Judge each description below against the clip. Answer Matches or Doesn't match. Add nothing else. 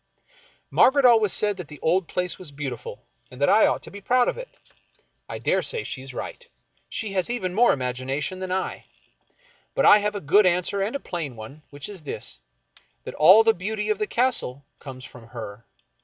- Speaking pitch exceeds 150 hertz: Matches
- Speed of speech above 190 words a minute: Matches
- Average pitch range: Doesn't match